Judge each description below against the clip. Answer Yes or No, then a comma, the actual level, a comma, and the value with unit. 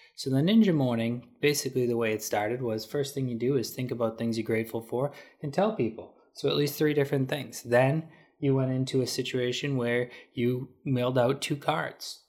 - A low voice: Yes, low, 130 Hz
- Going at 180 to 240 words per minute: Yes, fast, 205 wpm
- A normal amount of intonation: Yes, average, 3.0 semitones